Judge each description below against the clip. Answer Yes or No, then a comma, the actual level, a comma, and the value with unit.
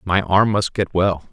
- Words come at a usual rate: No, fast, 225 wpm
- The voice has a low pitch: Yes, very low, 95 Hz